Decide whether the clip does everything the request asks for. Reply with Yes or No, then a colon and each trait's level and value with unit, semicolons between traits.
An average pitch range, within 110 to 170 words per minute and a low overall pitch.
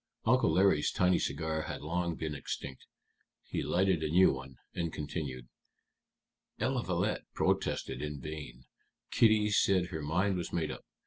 Yes: average, 3.8 semitones; average, 140 wpm; very low, 80 Hz